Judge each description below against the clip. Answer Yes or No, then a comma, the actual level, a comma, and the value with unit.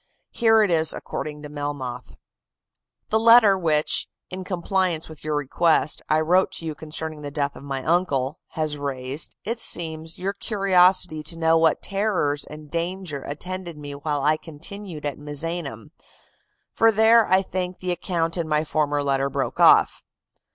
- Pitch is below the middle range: No, medium, 160 Hz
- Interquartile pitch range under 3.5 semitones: No, average, 4.0 semitones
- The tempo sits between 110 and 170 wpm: Yes, average, 160 wpm